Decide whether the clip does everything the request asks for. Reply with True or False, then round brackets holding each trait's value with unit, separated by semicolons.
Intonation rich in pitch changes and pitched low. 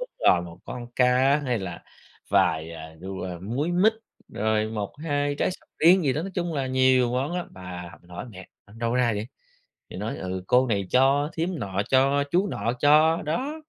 True (7.4 semitones; 125 Hz)